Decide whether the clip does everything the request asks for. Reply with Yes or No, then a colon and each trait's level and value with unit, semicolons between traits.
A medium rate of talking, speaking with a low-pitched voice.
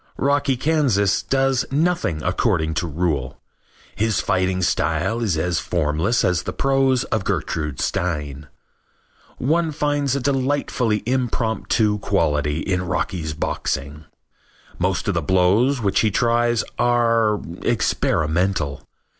No: slow, 115 wpm; low, 105 Hz